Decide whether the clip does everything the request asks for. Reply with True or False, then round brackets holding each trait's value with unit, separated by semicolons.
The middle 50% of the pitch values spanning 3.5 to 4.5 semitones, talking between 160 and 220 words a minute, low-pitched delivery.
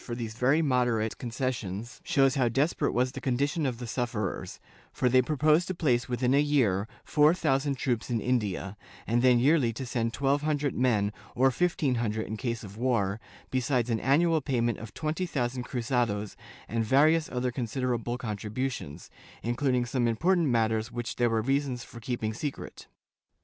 False (3.1 semitones; 170 wpm; 125 Hz)